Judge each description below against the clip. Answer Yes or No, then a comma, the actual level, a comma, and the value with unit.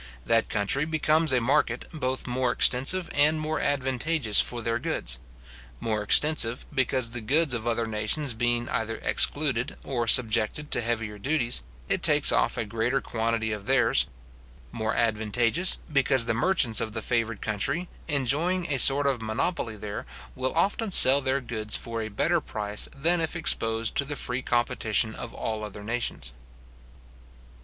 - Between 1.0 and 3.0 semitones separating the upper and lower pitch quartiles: No, average, 4.1 semitones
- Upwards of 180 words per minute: No, average, 160 wpm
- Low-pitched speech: Yes, low, 120 Hz